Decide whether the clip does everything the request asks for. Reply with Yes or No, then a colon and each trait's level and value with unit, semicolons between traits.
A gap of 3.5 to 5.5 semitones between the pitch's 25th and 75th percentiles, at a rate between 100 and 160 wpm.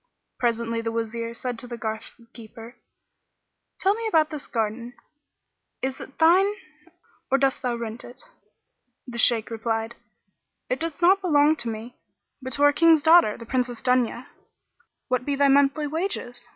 Yes: average, 4.0 semitones; average, 155 wpm